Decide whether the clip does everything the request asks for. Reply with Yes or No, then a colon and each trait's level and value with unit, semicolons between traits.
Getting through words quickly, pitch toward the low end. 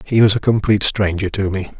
Yes: fast, 235 wpm; low, 100 Hz